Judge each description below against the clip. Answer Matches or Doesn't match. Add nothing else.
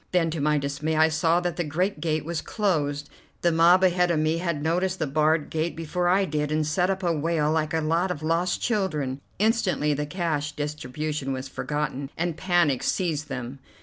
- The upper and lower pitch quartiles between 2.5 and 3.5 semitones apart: Matches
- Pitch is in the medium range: Matches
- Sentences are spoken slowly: Doesn't match